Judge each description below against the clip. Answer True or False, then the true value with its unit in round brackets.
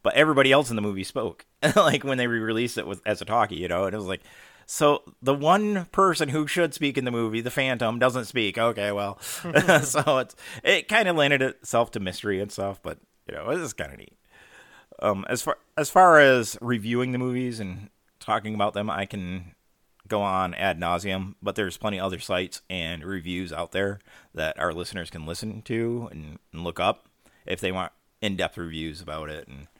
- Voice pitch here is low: True (110 Hz)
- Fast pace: True (210 wpm)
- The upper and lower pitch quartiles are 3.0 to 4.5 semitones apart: False (5.1 semitones)